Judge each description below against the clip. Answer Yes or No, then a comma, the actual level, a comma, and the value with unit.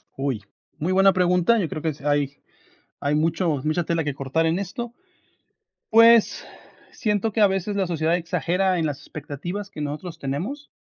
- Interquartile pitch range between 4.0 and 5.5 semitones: Yes, average, 4.6 semitones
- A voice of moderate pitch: Yes, medium, 170 Hz